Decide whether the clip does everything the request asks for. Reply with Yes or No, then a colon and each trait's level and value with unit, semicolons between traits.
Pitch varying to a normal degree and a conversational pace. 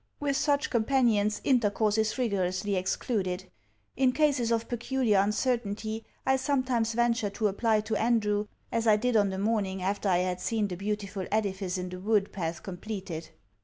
Yes: average, 3.2 semitones; average, 165 wpm